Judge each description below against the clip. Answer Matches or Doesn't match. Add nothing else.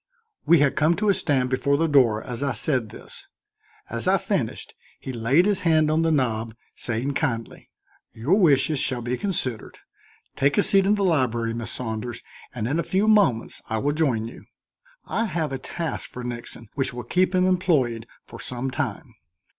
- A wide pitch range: Matches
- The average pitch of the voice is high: Doesn't match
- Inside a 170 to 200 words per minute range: Matches